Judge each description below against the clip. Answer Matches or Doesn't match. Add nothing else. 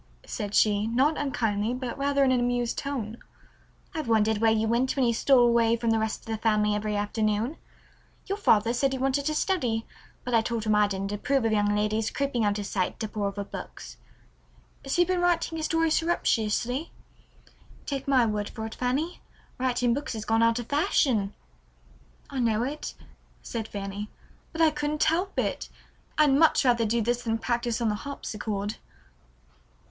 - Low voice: Doesn't match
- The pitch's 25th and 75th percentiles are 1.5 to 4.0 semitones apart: Doesn't match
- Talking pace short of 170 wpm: Doesn't match